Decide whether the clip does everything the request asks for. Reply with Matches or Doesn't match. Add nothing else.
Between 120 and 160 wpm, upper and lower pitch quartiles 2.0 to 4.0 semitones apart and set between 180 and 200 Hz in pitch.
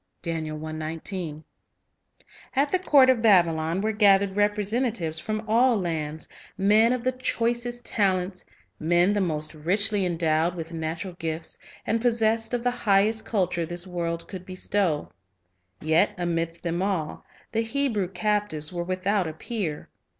Doesn't match